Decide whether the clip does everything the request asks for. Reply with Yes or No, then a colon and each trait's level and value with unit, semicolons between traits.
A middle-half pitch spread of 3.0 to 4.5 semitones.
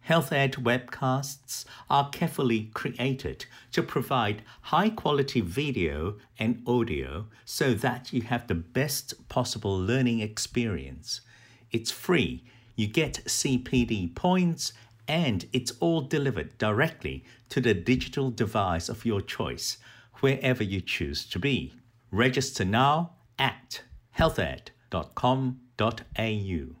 Yes: average, 3.4 semitones